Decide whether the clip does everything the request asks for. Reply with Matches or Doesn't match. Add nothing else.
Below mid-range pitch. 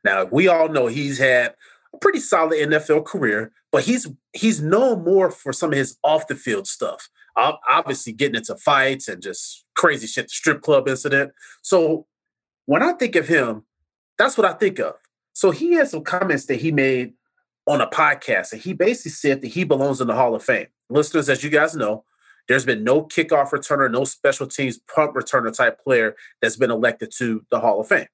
Doesn't match